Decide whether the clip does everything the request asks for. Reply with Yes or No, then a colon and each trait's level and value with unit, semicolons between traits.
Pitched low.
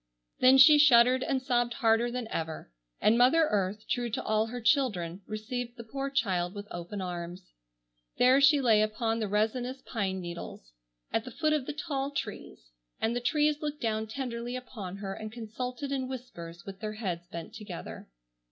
No: high, 230 Hz